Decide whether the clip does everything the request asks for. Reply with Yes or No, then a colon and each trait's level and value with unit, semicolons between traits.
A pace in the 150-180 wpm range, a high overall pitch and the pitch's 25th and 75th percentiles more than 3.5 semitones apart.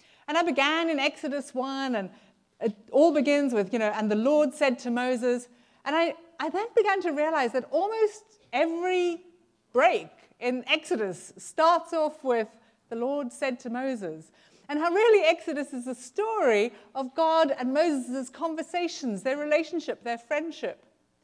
Yes: average, 160 wpm; very high, 280 Hz; average, 4.9 semitones